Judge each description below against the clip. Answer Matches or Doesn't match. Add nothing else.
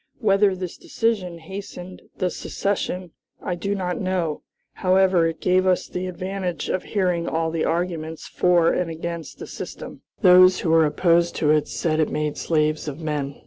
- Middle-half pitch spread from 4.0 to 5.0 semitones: Doesn't match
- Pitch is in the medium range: Matches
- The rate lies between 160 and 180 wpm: Matches